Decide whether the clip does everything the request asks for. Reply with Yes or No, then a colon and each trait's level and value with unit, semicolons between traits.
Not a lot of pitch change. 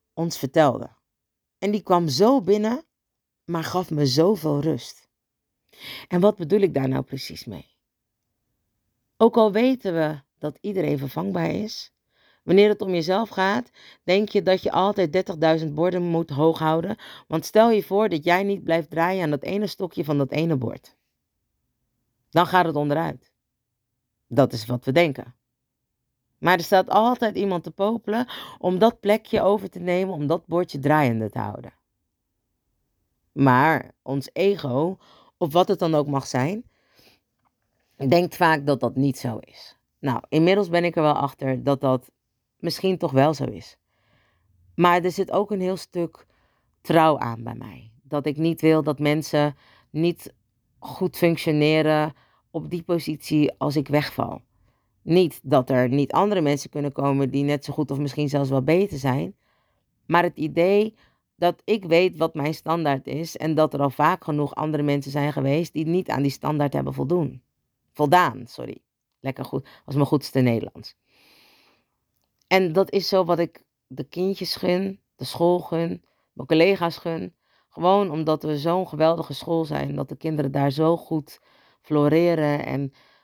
No: average, 4.8 semitones